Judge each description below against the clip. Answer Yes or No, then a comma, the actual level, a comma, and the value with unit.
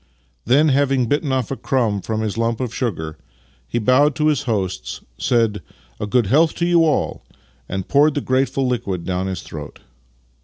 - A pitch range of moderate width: No, wide, 5.8 semitones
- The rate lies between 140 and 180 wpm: No, average, 190 wpm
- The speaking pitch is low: Yes, low, 120 Hz